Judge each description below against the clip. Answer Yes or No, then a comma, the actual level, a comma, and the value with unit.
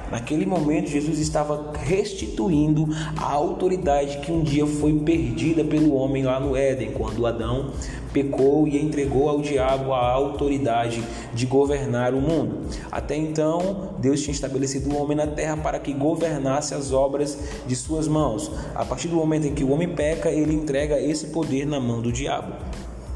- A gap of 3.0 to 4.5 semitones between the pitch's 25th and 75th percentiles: No, narrow, 2.4 semitones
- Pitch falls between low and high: Yes, medium, 145 Hz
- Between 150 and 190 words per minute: Yes, average, 170 wpm